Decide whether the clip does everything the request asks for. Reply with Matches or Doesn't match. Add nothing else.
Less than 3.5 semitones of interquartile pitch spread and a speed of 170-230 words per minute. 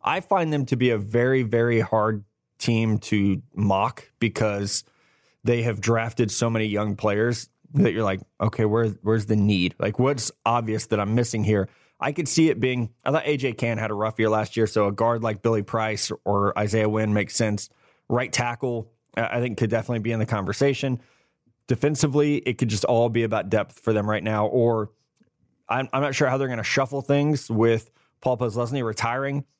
Matches